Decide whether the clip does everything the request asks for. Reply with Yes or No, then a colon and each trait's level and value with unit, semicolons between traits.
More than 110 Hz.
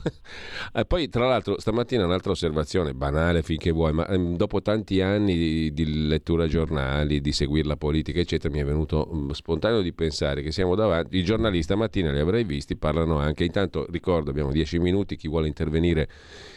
No: very low, 80 Hz